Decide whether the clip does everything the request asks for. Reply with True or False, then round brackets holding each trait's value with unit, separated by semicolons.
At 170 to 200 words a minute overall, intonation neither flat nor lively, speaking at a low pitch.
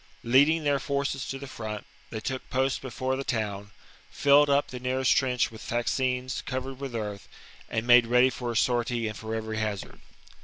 True (185 wpm; 3.1 semitones; 125 Hz)